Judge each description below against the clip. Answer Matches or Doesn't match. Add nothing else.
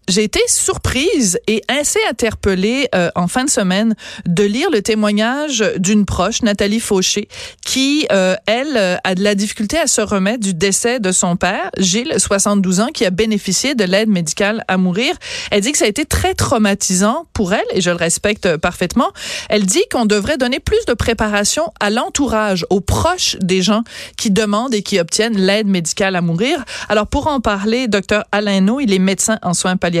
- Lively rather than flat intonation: Doesn't match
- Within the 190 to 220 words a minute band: Matches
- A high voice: Matches